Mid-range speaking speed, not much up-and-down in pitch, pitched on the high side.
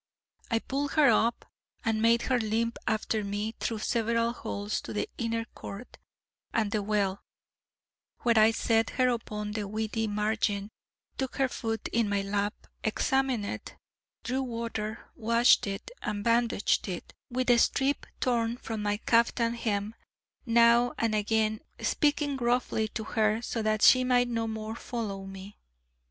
Yes: average, 150 wpm; narrow, 2.0 semitones; high, 225 Hz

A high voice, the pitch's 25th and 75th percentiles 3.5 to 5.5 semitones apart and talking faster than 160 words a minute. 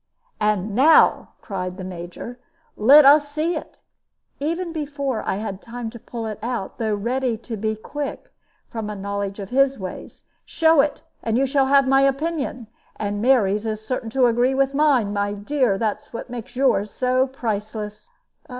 Yes: high, 235 Hz; average, 4.6 semitones; average, 170 wpm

